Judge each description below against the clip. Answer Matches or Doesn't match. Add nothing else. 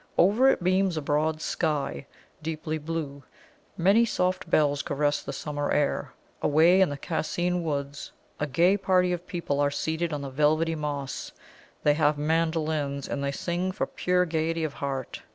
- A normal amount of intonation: Matches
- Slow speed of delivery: Doesn't match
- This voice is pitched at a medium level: Matches